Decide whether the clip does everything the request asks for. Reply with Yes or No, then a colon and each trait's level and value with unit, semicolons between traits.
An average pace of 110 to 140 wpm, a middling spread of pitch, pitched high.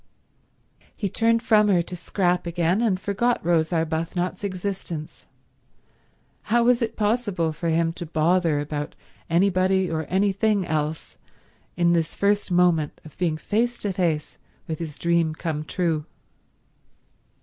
No: slow, 135 wpm; average, 3.8 semitones; medium, 175 Hz